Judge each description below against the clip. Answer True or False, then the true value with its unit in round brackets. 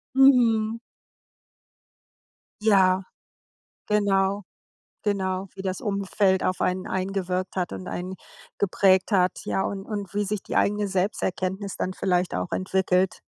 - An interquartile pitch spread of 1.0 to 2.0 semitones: True (1.5 semitones)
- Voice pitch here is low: False (190 Hz)